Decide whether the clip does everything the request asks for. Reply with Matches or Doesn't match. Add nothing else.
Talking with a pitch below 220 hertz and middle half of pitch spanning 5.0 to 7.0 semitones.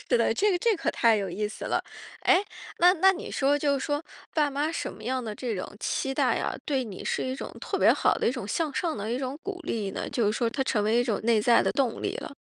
Doesn't match